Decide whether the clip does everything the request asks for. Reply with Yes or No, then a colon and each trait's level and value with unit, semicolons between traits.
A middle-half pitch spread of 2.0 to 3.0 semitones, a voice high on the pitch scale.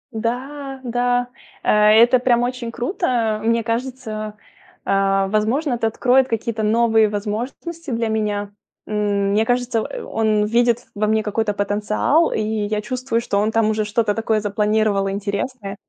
Yes: narrow, 2.6 semitones; high, 220 Hz